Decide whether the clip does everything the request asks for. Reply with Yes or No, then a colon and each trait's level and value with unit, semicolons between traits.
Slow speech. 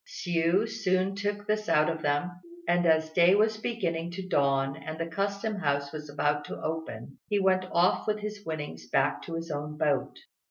No: average, 190 wpm